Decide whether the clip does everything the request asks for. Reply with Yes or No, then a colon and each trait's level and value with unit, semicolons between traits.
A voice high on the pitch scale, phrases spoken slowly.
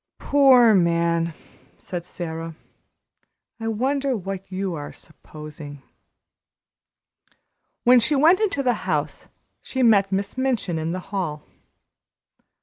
Yes: high, 195 Hz; slow, 110 wpm